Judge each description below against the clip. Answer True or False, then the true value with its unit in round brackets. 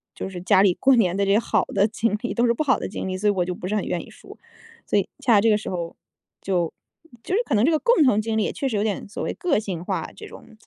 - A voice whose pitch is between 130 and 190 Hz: False (210 Hz)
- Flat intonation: False (3.8 semitones)